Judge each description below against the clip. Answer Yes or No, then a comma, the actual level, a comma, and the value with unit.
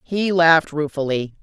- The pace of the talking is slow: Yes, slow, 125 wpm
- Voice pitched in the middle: Yes, medium, 155 Hz